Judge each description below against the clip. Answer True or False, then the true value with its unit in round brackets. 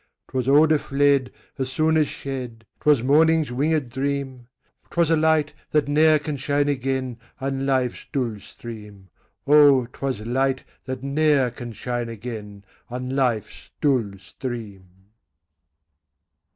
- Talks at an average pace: False (125 wpm)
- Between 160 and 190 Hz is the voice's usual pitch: False (135 Hz)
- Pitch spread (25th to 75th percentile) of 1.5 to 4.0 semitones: True (3.1 semitones)